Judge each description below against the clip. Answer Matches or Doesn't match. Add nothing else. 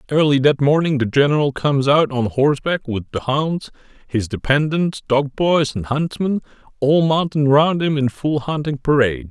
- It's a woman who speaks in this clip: Doesn't match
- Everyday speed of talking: Matches